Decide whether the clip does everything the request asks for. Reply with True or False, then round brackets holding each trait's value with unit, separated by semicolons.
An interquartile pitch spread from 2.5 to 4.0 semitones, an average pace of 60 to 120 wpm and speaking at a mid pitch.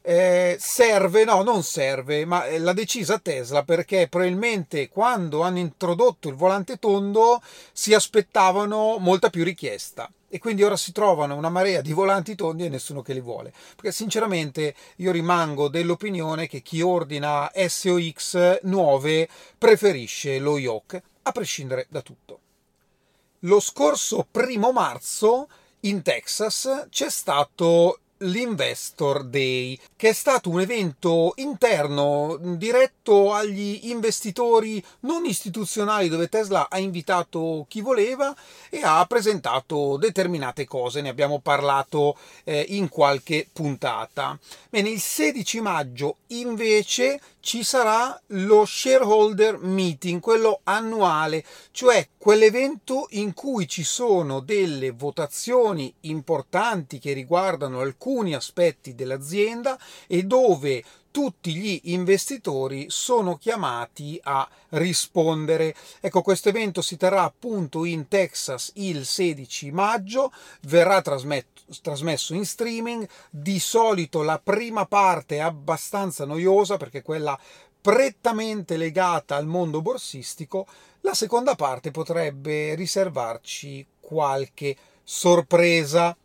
False (5.6 semitones; 115 wpm; 180 Hz)